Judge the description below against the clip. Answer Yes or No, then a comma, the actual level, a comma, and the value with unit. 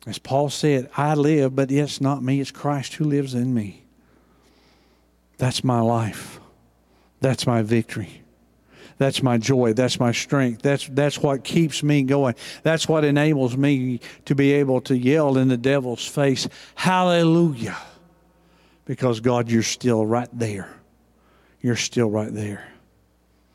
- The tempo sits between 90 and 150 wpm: Yes, average, 145 wpm